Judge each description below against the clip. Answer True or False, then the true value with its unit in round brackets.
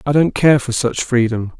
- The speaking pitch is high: False (130 Hz)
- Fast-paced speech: True (225 wpm)